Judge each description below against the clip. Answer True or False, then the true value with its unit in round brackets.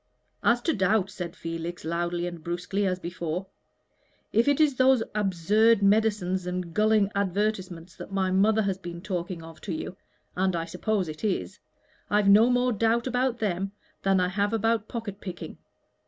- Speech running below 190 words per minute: True (170 wpm)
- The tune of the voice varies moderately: True (3.6 semitones)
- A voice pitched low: False (195 Hz)